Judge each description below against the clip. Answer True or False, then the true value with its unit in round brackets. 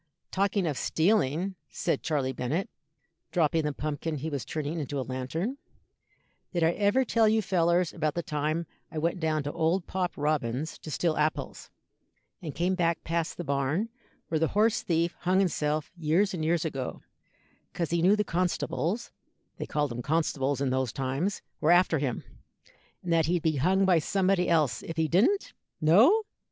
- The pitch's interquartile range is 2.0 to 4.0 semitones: True (3.6 semitones)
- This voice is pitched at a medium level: True (165 Hz)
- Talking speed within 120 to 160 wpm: False (175 wpm)